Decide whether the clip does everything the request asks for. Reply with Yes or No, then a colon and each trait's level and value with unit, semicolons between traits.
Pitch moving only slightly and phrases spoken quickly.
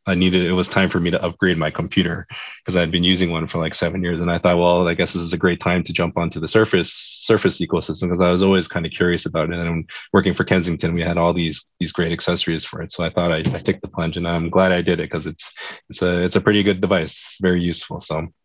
Yes: narrow, 1.3 semitones; fast, 285 wpm